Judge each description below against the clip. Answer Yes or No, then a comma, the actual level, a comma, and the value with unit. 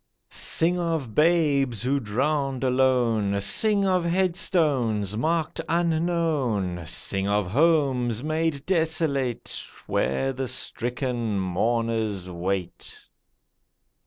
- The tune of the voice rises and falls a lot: Yes, wide, 6.8 semitones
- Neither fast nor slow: No, slow, 90 wpm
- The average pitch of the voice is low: Yes, low, 130 Hz